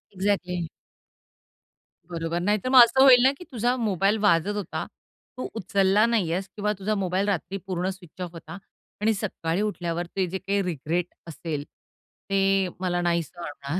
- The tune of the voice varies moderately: Yes, average, 3.1 semitones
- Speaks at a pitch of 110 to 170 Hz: No, high, 190 Hz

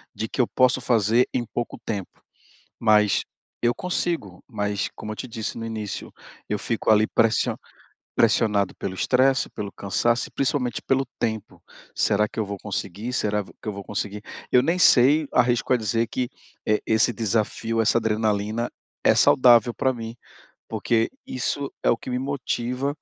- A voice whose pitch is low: Yes, low, 115 Hz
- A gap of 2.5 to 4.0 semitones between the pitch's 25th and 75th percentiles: Yes, average, 2.9 semitones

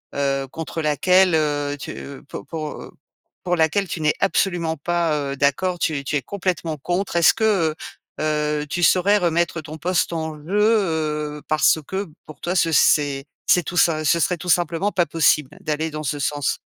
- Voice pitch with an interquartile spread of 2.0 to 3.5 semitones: Yes, average, 2.9 semitones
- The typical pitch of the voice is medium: Yes, medium, 160 Hz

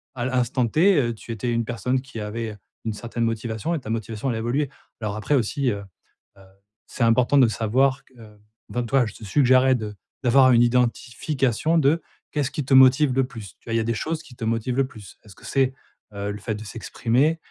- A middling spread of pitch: Yes, average, 3.0 semitones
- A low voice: Yes, low, 120 Hz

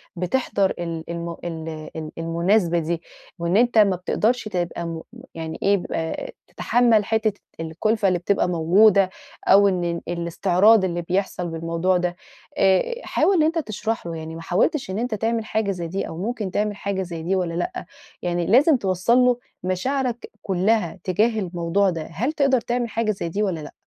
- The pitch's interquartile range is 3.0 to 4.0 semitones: No, average, 4.5 semitones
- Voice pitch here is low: No, high, 190 Hz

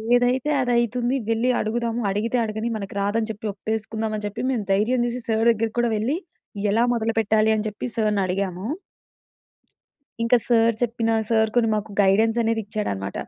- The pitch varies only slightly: Yes, narrow, 1.8 semitones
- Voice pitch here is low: No, high, 220 Hz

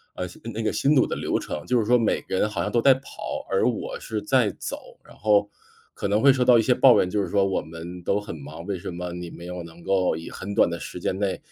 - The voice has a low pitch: Yes, low, 100 Hz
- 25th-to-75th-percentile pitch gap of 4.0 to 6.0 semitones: Yes, average, 4.5 semitones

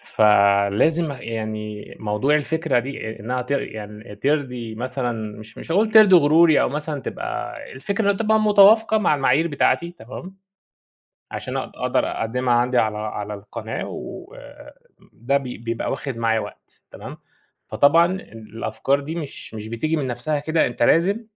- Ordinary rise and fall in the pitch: No, wide, 6.4 semitones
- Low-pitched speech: Yes, low, 130 Hz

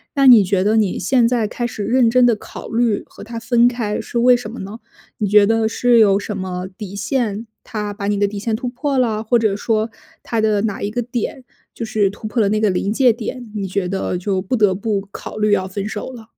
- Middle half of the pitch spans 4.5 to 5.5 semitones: No, average, 2.8 semitones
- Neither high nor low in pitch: No, high, 215 Hz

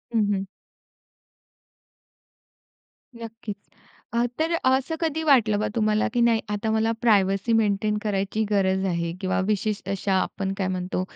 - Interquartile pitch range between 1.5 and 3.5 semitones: Yes, average, 2.8 semitones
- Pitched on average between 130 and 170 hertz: No, high, 210 Hz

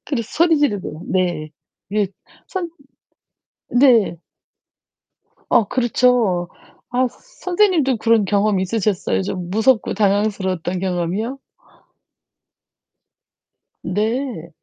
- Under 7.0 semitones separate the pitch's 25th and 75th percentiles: Yes, average, 5.2 semitones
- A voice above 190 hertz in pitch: Yes, high, 215 Hz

